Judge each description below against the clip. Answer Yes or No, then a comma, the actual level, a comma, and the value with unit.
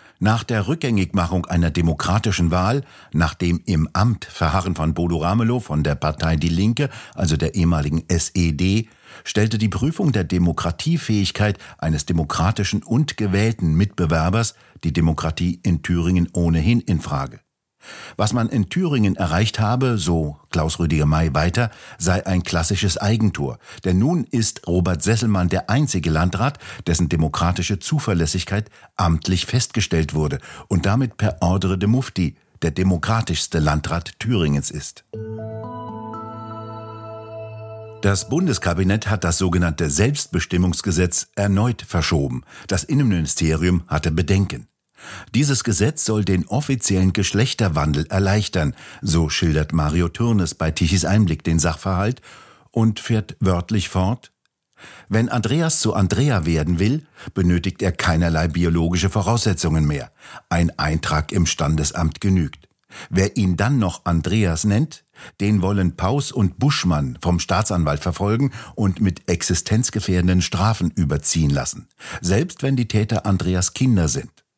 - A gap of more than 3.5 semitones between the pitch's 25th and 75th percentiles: Yes, average, 4.6 semitones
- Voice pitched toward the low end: Yes, very low, 95 Hz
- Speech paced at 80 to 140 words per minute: Yes, slow, 125 wpm